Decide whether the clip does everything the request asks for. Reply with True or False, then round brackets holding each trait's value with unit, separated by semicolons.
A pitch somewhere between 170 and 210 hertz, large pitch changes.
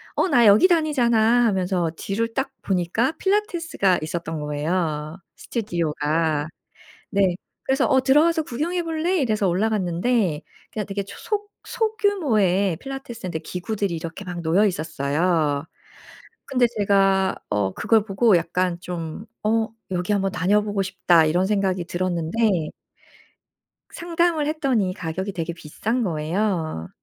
True (195 Hz; 5.9 semitones)